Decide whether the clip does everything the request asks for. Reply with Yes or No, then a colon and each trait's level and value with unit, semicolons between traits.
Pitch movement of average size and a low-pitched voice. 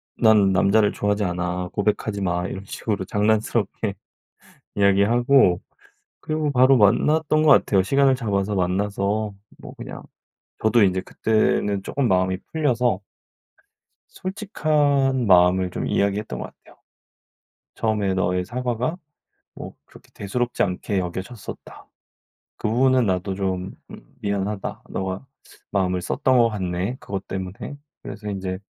Yes: average, 4.5 semitones; low, 105 Hz